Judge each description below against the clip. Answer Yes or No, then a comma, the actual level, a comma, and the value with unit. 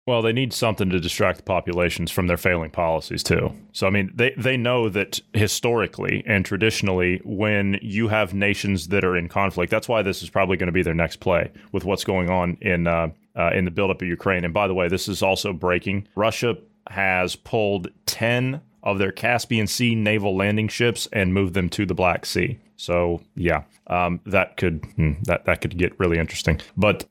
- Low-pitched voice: Yes, low, 100 Hz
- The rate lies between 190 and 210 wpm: Yes, fast, 205 wpm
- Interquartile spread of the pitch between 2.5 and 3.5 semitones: Yes, average, 3.2 semitones